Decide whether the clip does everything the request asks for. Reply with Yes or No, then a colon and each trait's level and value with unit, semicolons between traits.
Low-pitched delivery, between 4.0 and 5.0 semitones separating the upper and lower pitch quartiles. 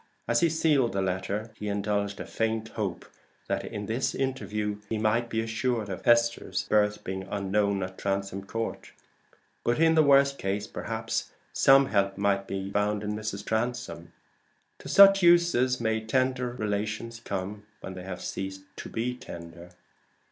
No: low, 105 Hz; average, 3.5 semitones